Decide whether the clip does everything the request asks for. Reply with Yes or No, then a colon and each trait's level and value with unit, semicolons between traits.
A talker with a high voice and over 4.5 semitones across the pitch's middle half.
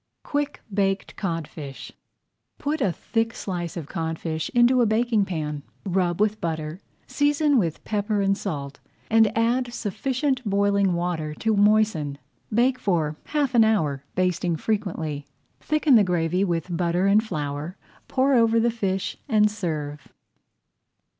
Yes: high, 195 Hz; wide, 5.5 semitones